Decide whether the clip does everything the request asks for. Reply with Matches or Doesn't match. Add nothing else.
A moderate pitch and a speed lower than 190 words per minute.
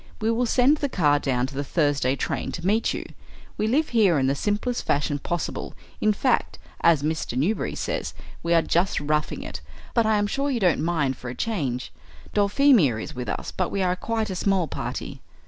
Doesn't match